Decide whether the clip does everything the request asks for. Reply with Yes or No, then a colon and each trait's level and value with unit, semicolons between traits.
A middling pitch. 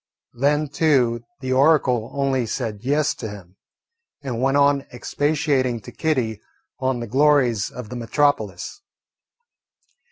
No: low, 130 Hz